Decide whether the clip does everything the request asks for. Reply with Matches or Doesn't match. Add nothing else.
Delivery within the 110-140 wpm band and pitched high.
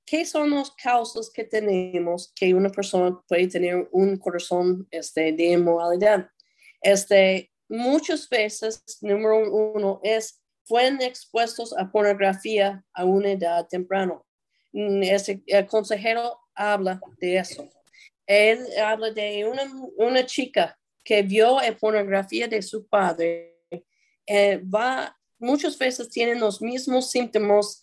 Matches